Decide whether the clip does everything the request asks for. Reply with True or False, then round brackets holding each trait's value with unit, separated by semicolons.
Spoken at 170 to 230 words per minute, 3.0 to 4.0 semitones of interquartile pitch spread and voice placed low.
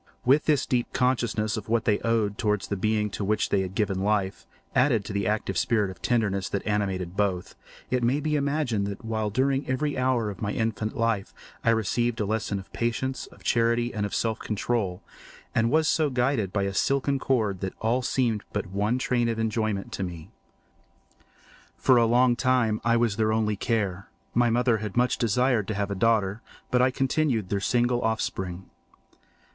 True (190 wpm; 3.3 semitones; 110 Hz)